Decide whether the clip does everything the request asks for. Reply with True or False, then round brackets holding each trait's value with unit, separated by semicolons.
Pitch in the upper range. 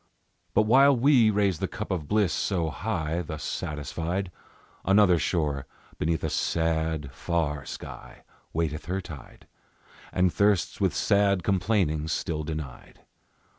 False (85 Hz)